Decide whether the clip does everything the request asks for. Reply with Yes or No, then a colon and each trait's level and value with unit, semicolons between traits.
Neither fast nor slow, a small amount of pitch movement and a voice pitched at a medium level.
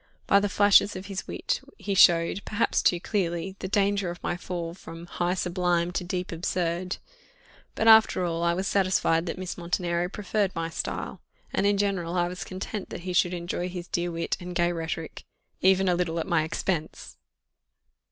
Yes: average, 185 wpm; narrow, 1.9 semitones; medium, 180 Hz